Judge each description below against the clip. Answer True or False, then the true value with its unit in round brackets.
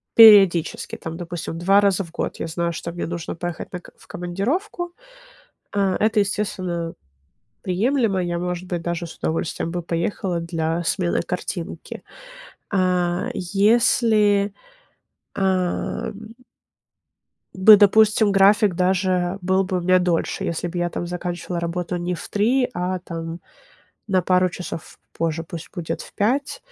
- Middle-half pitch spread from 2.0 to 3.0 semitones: True (2.7 semitones)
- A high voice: False (180 Hz)